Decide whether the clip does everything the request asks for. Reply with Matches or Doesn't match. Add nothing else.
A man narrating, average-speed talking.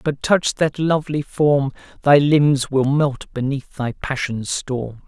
Matches